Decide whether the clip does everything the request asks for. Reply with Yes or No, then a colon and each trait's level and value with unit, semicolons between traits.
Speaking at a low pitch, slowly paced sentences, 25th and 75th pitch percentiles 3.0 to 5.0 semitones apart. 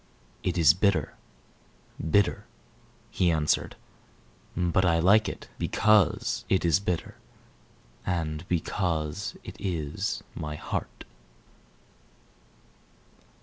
Yes: very low, 85 Hz; slow, 90 wpm; average, 3.6 semitones